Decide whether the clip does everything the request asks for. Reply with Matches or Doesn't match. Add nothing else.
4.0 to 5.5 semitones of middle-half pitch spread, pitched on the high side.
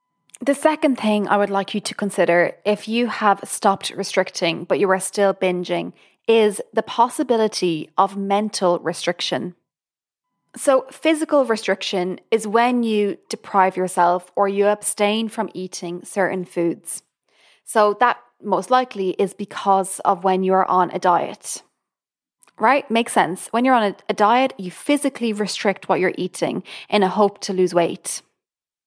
Doesn't match